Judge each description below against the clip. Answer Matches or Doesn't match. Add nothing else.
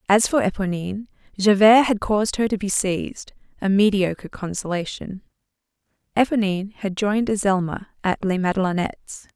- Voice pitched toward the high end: Matches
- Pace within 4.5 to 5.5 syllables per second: Doesn't match